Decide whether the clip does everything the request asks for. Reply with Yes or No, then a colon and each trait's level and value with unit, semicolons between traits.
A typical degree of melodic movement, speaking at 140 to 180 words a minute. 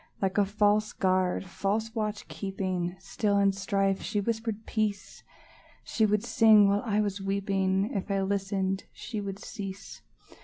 No: narrow, 1.5 semitones; average, 150 wpm